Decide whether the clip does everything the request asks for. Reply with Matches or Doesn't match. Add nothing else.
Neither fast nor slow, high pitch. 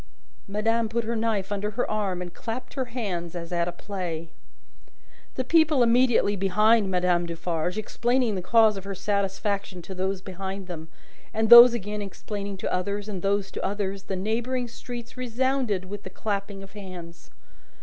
Matches